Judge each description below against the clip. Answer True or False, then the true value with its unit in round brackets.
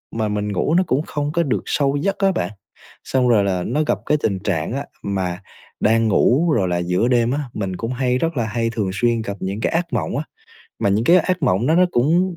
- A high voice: False (120 Hz)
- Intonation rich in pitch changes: True (6.8 semitones)